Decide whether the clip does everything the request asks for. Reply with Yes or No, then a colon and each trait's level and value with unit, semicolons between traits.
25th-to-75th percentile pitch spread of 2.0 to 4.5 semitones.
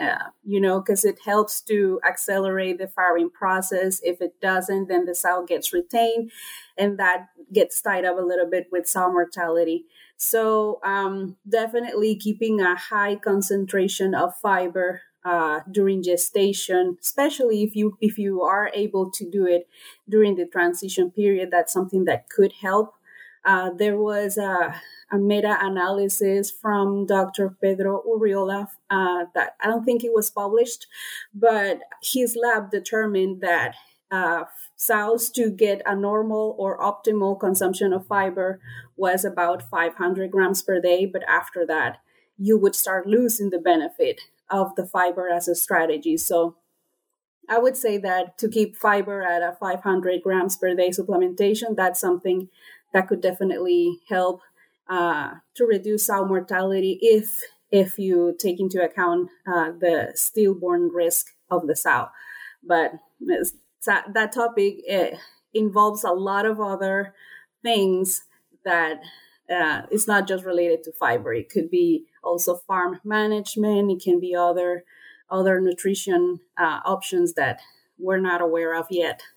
Yes: average, 2.7 semitones